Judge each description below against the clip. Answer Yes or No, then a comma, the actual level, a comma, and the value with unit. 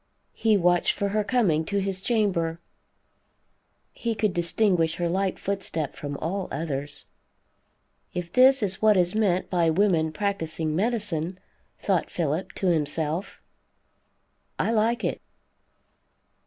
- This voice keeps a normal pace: No, slow, 125 wpm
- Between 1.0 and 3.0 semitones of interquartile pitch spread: No, average, 4.1 semitones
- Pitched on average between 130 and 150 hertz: No, medium, 185 Hz